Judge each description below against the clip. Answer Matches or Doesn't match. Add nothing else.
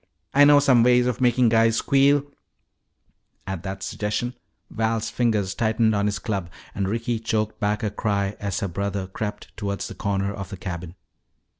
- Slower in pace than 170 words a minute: Doesn't match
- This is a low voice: Matches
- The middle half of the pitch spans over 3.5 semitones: Doesn't match